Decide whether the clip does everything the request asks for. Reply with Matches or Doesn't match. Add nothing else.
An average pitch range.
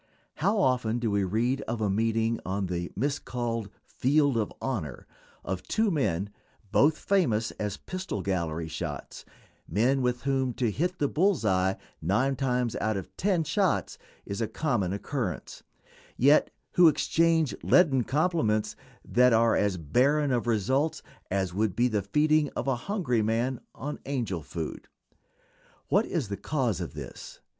Doesn't match